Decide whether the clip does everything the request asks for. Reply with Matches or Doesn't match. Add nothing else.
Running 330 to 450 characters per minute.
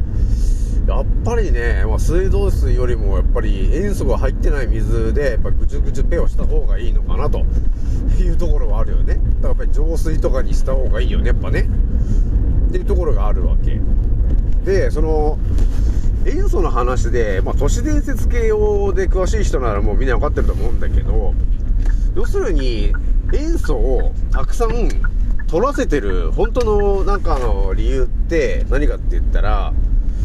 Matches